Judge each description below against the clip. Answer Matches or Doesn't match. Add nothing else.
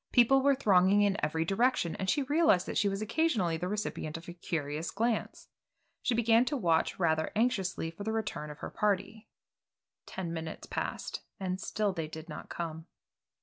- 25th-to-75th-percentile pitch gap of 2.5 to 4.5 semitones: Doesn't match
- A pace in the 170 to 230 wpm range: Matches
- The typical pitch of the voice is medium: Doesn't match